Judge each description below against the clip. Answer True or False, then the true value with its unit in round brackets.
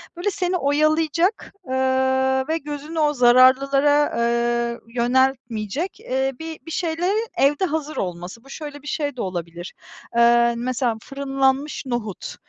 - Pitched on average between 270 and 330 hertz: True (275 Hz)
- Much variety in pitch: False (4.5 semitones)